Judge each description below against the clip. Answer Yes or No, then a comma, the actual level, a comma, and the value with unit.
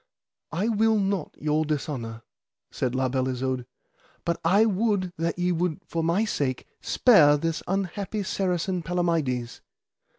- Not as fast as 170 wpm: Yes, slow, 135 wpm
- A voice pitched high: No, medium, 170 Hz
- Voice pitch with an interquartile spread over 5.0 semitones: Yes, wide, 5.4 semitones